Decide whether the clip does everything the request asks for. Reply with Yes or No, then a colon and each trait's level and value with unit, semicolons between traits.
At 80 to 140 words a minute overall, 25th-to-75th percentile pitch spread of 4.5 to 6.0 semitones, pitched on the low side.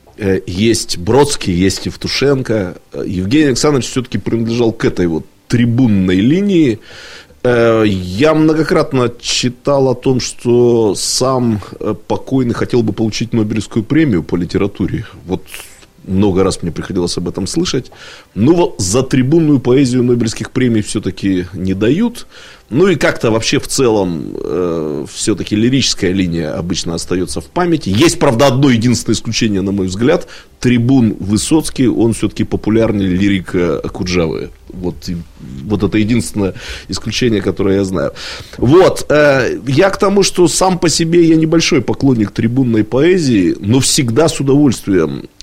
Yes: average, 135 wpm; wide, 5.5 semitones; low, 115 Hz